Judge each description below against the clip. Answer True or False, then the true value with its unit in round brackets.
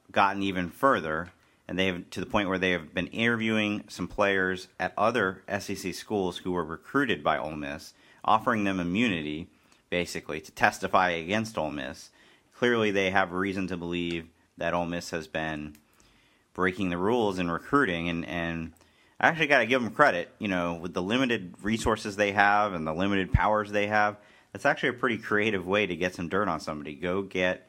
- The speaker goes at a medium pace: True (190 wpm)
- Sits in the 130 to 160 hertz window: False (95 Hz)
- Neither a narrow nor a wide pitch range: True (3.2 semitones)